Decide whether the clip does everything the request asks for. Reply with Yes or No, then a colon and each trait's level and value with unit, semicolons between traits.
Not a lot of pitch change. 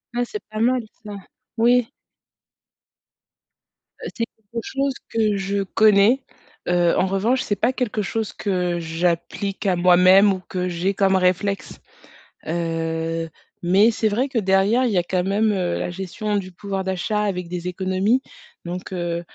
No: average, 3.3 semitones